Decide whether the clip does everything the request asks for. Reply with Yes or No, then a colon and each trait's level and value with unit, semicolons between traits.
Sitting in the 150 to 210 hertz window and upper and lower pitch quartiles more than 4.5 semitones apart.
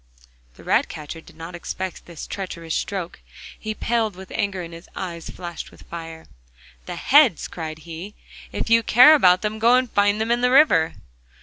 Yes: high, 190 Hz; average, 5.1 semitones